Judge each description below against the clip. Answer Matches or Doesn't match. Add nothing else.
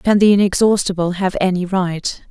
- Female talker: Matches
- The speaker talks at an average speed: Matches